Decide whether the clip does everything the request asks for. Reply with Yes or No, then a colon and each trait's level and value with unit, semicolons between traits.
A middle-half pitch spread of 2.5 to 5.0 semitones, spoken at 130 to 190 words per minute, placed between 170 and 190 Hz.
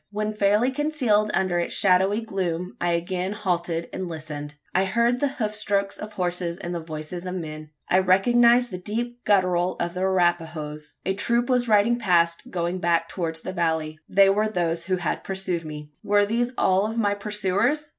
Yes: average, 3.6 semitones; average, 185 wpm; medium, 185 Hz